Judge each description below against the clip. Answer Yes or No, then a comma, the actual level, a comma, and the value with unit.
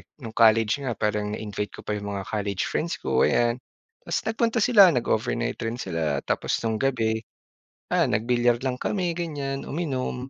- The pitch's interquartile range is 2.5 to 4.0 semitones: No, average, 4.4 semitones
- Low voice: Yes, low, 120 Hz